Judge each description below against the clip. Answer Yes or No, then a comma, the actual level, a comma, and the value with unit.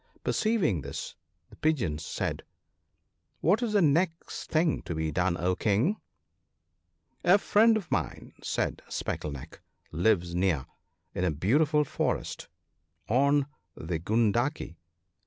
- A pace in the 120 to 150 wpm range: Yes, average, 140 wpm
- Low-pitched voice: Yes, low, 110 Hz